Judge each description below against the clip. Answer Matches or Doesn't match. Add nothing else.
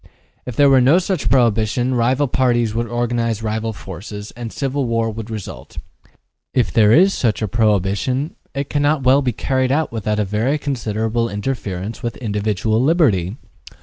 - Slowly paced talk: Doesn't match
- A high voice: Doesn't match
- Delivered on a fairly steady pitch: Doesn't match